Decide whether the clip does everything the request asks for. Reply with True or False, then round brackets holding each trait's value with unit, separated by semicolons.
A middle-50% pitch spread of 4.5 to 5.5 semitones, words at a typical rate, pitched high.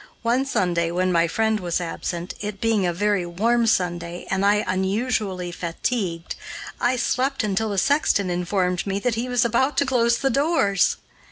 True (4.8 semitones; 170 wpm; 200 Hz)